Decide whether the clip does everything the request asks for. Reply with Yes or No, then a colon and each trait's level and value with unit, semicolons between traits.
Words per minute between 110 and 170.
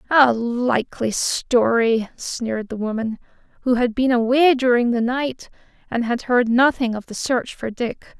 Yes: average, 160 wpm